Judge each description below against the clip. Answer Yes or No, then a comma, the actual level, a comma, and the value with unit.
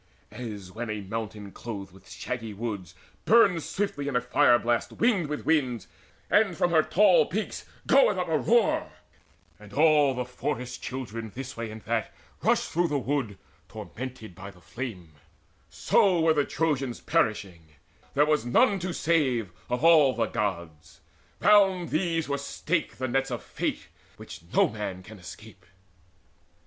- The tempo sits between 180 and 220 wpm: No, average, 155 wpm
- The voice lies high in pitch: No, low, 125 Hz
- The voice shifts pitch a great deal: Yes, wide, 6.8 semitones